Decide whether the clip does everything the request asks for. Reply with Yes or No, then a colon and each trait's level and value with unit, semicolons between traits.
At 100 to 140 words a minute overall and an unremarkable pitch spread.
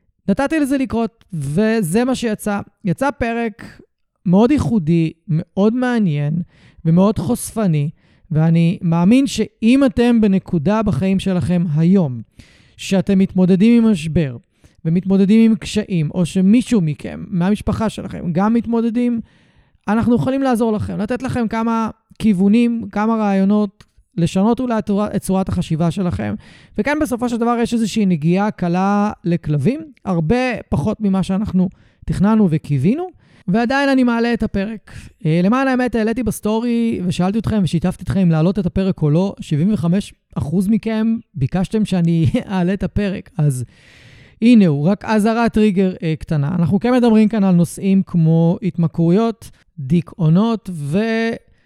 Yes: average, 130 wpm; average, 4.5 semitones